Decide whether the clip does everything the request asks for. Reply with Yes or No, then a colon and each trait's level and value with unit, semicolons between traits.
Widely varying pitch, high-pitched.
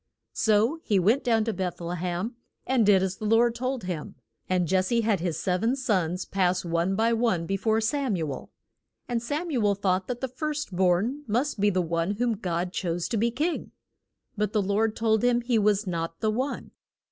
No: average, 4.4 semitones; high, 210 Hz